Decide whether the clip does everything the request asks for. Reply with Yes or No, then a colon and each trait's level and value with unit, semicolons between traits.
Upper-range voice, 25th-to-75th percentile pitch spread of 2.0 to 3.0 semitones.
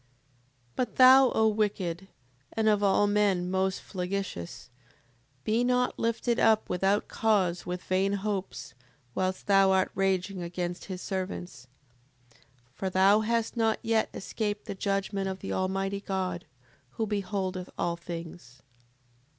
Yes: high, 195 Hz; narrow, 2.5 semitones